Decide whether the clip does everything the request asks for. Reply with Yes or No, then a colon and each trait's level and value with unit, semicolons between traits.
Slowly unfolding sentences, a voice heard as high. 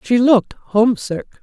Yes: slow, 125 wpm; high, 225 Hz